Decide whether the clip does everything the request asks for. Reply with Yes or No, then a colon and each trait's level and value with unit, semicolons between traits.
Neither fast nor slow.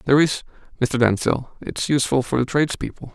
Yes: average, 190 wpm